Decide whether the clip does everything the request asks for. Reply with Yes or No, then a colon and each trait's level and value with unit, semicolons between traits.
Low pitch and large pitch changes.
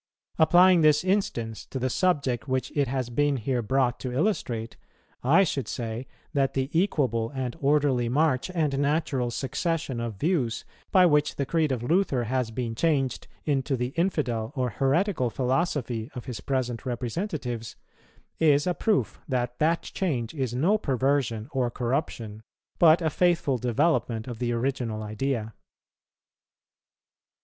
No: low, 130 Hz; average, 4.3 semitones